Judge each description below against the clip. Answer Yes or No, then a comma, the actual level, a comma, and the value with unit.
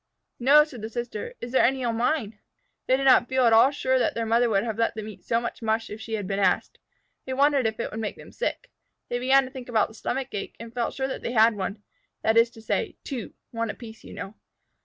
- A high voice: Yes, high, 235 Hz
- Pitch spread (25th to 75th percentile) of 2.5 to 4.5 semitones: Yes, average, 2.9 semitones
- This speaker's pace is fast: Yes, fast, 260 wpm